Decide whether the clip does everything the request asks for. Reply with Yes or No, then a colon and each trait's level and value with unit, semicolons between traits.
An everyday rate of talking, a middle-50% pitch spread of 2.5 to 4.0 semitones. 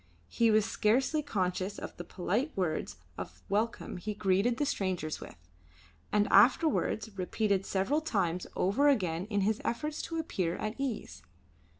No: average, 150 wpm; average, 4.6 semitones